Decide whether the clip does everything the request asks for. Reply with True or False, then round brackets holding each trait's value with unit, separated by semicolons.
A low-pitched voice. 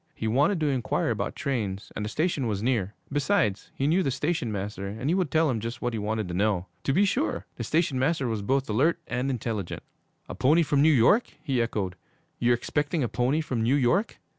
True (130 Hz)